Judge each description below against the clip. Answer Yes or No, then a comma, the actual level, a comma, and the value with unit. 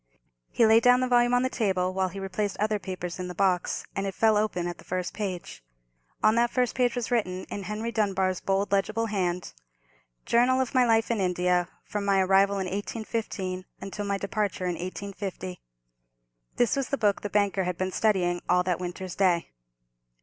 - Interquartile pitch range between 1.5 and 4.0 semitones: Yes, average, 3.3 semitones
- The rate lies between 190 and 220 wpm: Yes, average, 195 wpm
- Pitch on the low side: No, high, 195 Hz